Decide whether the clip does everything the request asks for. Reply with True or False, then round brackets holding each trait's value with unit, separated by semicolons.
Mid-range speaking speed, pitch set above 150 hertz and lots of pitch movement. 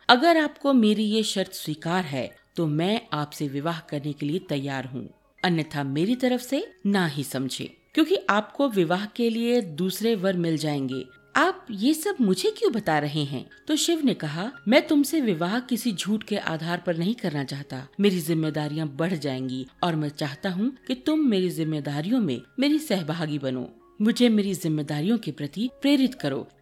True (175 wpm; 185 Hz; 8.0 semitones)